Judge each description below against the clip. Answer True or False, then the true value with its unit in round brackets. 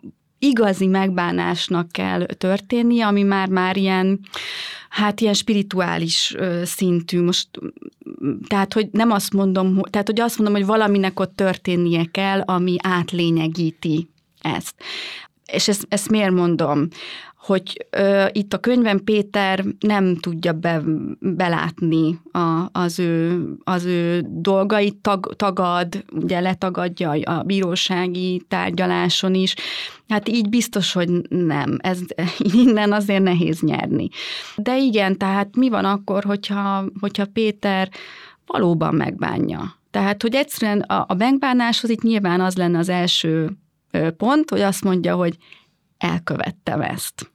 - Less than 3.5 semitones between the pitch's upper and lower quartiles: True (2.8 semitones)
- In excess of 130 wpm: False (125 wpm)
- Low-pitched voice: False (190 Hz)